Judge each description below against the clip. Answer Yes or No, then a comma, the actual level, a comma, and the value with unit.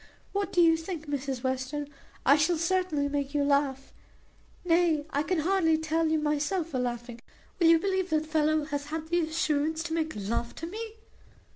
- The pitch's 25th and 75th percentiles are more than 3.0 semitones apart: No, average, 2.7 semitones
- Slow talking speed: No, average, 185 wpm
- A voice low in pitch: No, very high, 310 Hz